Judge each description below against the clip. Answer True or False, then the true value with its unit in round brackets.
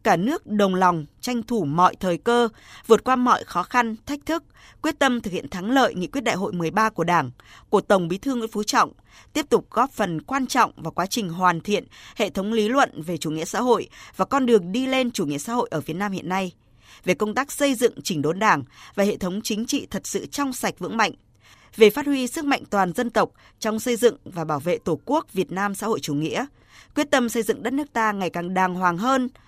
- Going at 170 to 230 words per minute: False (250 wpm)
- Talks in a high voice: True (215 Hz)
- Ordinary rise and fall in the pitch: False (5.7 semitones)